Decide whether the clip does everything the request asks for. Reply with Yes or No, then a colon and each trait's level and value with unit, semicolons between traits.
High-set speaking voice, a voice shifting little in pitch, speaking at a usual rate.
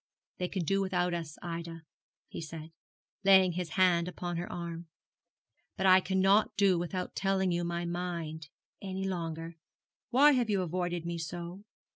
No: medium, 175 Hz; narrow, 2.1 semitones; average, 155 wpm